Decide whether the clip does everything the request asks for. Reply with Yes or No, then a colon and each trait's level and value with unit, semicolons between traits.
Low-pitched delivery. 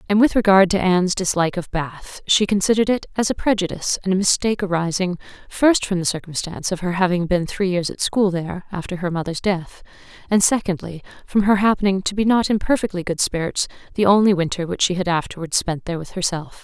No: medium, 185 Hz